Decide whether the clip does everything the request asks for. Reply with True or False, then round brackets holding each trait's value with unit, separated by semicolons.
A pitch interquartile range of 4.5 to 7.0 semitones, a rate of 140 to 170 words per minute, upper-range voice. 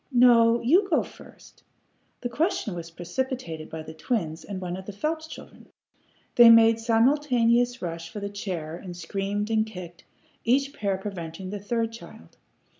True (5.3 semitones; 160 wpm; 210 Hz)